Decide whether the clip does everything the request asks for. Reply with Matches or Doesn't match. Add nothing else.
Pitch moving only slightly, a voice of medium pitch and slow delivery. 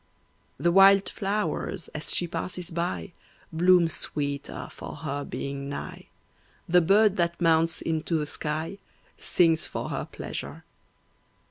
Doesn't match